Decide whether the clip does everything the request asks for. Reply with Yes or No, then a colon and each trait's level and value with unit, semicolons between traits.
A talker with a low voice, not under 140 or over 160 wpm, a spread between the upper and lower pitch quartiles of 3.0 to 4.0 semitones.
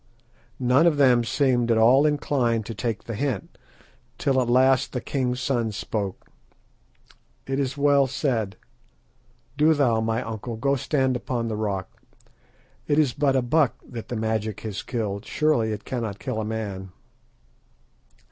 Yes: low, 120 Hz; average, 155 wpm; average, 3.5 semitones